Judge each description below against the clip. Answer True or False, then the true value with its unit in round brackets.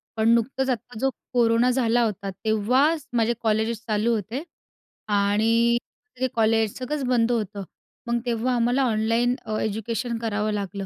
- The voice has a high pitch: True (230 Hz)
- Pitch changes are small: True (2.0 semitones)